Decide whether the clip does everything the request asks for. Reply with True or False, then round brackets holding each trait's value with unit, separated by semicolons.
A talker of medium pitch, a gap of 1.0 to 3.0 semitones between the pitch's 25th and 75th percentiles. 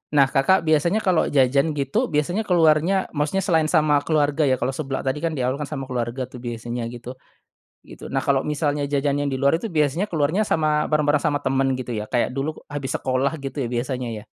True (145 Hz; 2.7 semitones)